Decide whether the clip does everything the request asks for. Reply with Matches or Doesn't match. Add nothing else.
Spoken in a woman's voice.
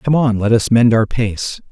Doesn't match